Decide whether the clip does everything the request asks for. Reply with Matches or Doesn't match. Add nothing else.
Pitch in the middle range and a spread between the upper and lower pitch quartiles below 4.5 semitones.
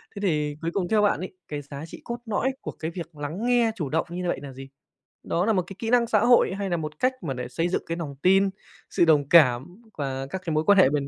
Doesn't match